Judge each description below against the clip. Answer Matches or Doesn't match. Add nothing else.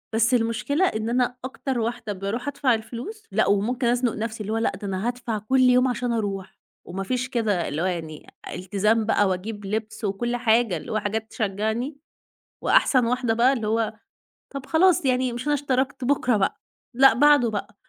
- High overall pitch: Matches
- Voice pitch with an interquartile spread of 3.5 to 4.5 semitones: Doesn't match